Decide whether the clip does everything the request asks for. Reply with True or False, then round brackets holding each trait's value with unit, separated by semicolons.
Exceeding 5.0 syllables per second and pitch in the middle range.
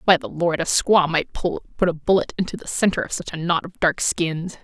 True (5.2 syllables/s; 170 Hz)